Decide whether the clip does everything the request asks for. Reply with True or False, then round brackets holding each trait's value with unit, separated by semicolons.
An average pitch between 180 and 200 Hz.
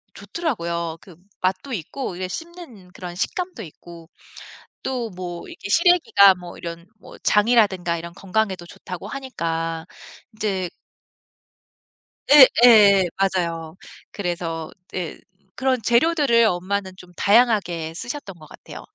True (190 Hz)